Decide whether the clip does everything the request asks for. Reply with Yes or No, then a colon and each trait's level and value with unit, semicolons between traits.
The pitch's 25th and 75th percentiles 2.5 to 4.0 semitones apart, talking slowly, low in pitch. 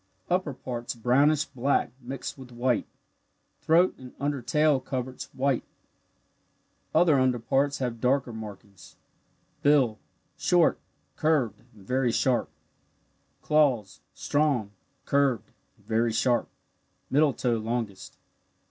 Yes: average, 3.3 semitones; slow, 110 wpm; low, 130 Hz